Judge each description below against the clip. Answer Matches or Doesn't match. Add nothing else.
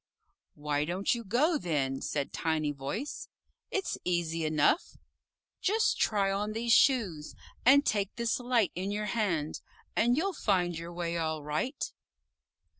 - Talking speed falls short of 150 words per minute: Matches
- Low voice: Doesn't match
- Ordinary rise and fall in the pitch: Doesn't match